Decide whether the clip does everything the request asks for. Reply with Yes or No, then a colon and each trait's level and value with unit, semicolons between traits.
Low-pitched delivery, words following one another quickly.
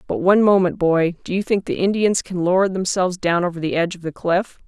No: medium, 180 Hz; fast, 245 wpm